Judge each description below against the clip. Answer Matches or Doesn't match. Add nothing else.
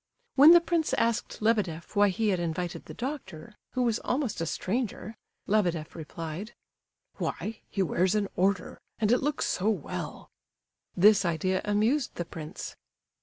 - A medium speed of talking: Matches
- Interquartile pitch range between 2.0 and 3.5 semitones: Doesn't match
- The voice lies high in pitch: Matches